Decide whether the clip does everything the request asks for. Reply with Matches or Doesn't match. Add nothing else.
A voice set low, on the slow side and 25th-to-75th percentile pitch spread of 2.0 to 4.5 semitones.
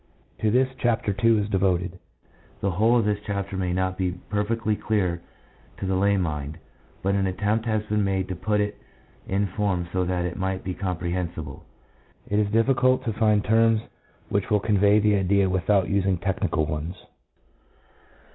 Doesn't match